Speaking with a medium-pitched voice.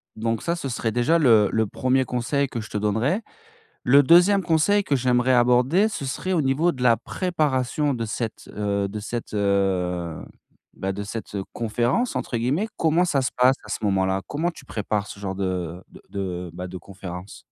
No: low, 120 Hz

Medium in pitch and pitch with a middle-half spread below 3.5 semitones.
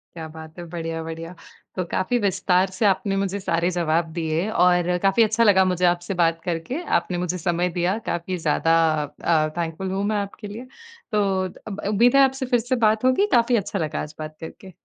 No: medium, 180 Hz; average, 3.8 semitones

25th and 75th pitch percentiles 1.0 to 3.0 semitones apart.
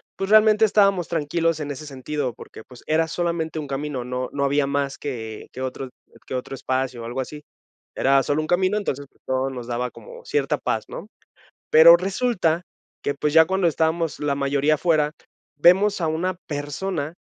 No: average, 4.2 semitones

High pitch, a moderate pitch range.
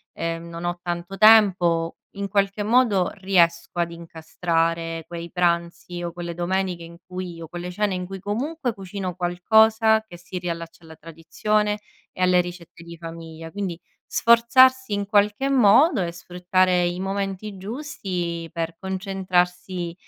No: medium, 180 Hz; average, 3.0 semitones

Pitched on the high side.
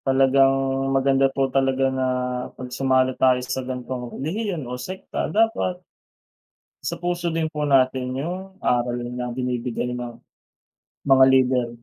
No: low, 130 Hz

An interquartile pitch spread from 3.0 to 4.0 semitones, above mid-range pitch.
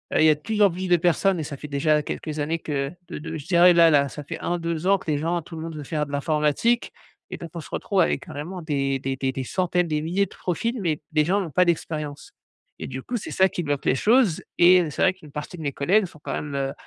No: average, 3.5 semitones; medium, 160 Hz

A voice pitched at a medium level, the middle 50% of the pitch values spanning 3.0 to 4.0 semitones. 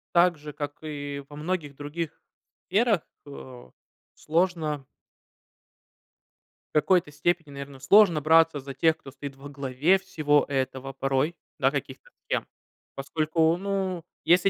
Yes: medium, 150 Hz; average, 3.6 semitones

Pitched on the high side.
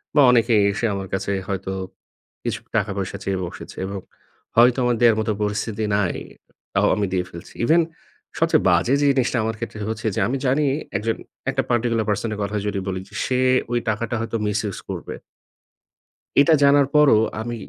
No: low, 110 Hz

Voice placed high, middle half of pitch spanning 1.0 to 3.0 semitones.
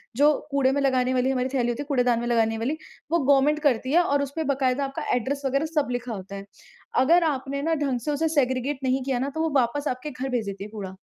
Yes: very high, 265 Hz; narrow, 2.6 semitones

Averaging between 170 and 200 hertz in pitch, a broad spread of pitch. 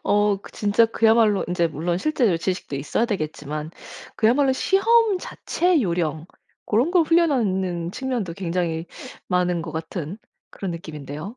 Yes: high, 190 Hz; wide, 6.1 semitones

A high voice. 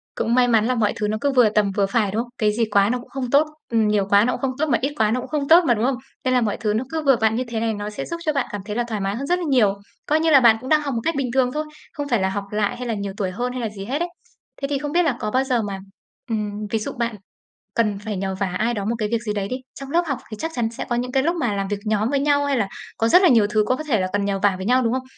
Yes: high, 235 Hz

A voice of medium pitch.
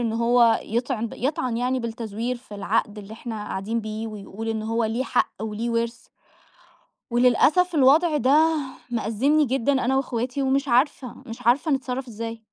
No: high, 235 Hz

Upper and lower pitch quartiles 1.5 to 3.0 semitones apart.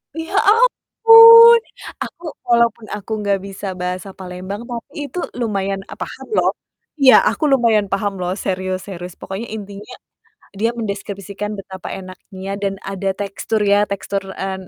No: average, 3.5 semitones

